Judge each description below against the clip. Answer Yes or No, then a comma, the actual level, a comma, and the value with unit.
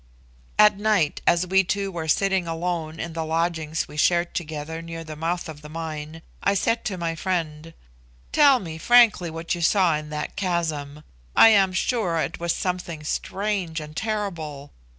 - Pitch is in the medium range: Yes, medium, 170 Hz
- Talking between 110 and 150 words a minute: No, average, 170 wpm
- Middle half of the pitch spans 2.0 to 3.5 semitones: Yes, average, 3.2 semitones